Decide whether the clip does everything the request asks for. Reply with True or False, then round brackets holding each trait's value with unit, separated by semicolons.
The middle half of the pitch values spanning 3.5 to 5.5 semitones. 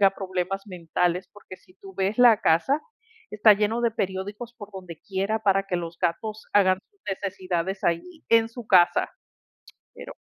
False (2.8 semitones)